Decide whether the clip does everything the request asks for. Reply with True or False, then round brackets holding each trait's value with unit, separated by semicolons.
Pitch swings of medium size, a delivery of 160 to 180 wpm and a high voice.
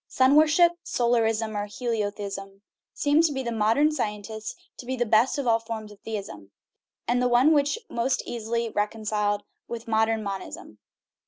True (3.2 semitones; 165 wpm; 225 Hz)